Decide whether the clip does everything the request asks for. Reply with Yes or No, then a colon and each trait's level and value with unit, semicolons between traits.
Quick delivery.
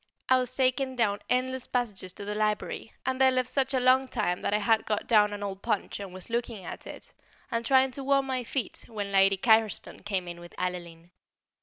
Yes: fast, 215 wpm